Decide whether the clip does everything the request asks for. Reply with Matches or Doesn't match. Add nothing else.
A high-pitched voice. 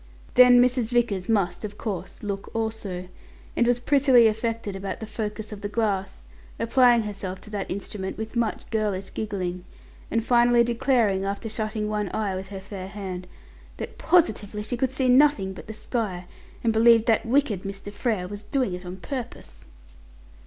Matches